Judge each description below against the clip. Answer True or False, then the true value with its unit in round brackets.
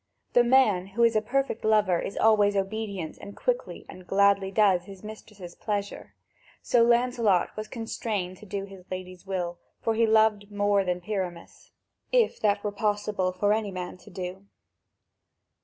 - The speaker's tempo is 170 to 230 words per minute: False (160 wpm)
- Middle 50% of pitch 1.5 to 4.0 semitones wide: True (2.8 semitones)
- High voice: True (205 Hz)